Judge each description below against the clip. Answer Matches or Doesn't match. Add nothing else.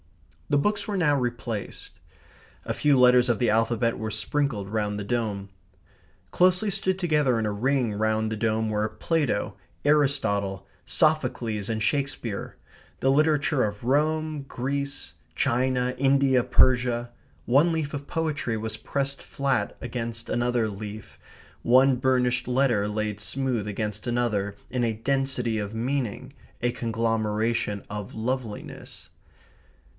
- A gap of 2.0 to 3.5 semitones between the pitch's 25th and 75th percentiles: Doesn't match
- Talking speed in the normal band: Doesn't match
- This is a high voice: Doesn't match